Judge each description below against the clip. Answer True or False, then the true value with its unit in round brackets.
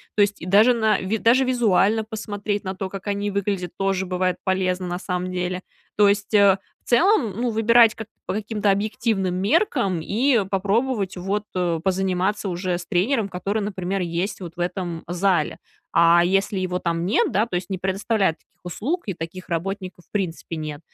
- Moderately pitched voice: False (195 Hz)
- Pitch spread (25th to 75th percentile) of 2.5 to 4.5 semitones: True (2.8 semitones)